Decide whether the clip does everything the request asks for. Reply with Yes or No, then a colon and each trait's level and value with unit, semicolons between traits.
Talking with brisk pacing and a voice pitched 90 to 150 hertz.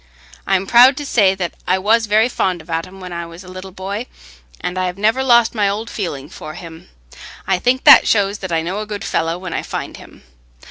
No: fast, 225 wpm; high, 190 Hz